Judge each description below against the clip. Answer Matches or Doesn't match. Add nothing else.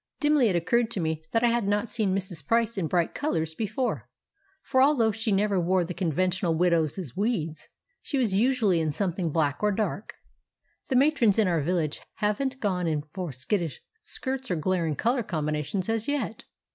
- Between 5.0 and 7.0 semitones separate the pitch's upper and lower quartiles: Matches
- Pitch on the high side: Matches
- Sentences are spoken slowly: Doesn't match